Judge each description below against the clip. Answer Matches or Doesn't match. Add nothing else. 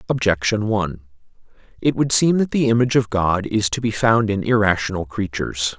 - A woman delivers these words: Doesn't match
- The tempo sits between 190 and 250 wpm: Doesn't match